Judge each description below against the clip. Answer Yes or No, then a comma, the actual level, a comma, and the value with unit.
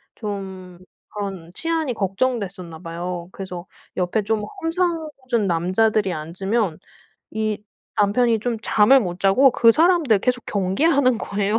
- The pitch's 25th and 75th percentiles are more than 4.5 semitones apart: Yes, average, 5.1 semitones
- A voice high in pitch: Yes, high, 210 Hz